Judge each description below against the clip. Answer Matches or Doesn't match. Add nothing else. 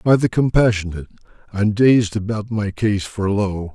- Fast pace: Doesn't match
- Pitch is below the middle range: Matches